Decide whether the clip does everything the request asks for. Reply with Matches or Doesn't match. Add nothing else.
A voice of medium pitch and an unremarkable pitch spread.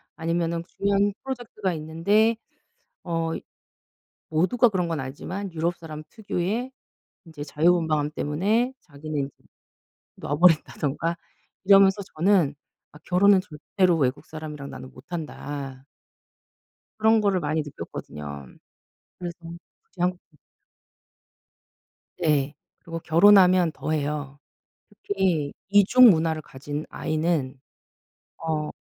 Matches